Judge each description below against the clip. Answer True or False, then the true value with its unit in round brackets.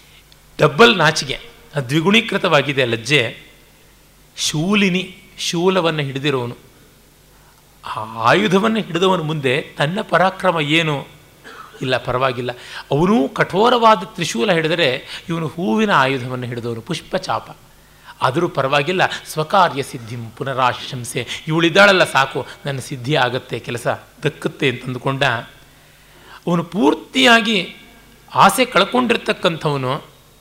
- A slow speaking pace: False (85 wpm)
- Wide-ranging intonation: True (5.8 semitones)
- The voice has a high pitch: False (155 Hz)